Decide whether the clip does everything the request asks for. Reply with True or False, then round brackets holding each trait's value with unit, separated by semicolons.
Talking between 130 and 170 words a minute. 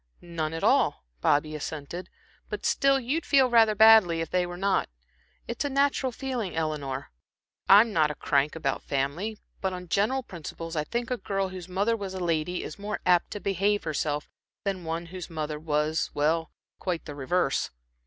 False (180 wpm)